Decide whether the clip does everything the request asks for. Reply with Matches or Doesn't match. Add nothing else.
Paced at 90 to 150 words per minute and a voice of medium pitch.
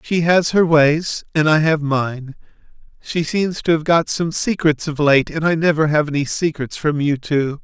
Doesn't match